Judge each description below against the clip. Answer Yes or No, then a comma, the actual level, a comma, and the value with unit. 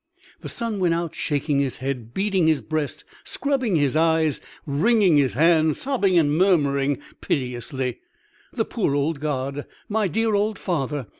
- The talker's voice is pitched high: No, medium, 155 Hz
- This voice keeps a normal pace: Yes, average, 150 wpm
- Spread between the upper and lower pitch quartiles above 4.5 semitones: Yes, wide, 5.5 semitones